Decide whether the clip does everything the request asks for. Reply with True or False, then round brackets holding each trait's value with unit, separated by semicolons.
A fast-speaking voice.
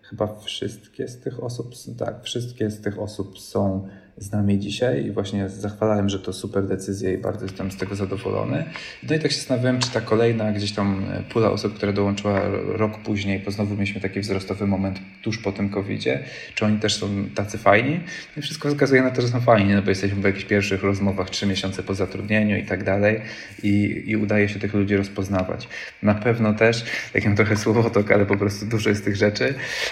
True (205 wpm)